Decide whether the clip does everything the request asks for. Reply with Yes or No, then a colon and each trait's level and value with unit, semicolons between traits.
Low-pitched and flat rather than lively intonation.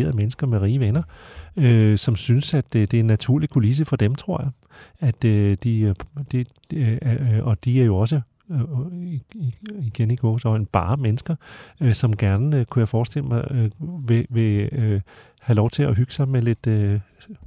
No: low, 120 Hz; average, 3.8 semitones